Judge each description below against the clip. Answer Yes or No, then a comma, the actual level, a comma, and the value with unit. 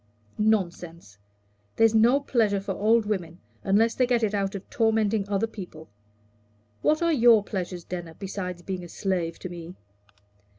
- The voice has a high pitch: Yes, high, 200 Hz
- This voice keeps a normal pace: Yes, average, 155 wpm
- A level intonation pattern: No, average, 3.9 semitones